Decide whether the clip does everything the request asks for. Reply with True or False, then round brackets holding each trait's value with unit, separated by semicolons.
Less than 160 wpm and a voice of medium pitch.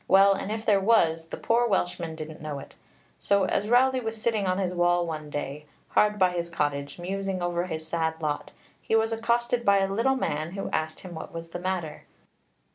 False (205 wpm; 180 Hz)